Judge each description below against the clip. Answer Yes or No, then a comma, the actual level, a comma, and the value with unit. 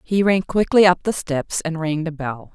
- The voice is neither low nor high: Yes, medium, 170 Hz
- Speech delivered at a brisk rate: Yes, fast, 235 wpm